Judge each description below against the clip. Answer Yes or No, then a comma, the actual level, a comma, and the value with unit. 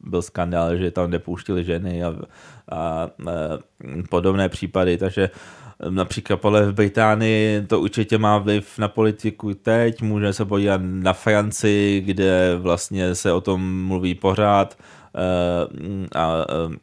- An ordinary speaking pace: Yes, average, 130 wpm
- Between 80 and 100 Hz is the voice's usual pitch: Yes, very low, 95 Hz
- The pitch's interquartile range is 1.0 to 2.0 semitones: No, average, 2.7 semitones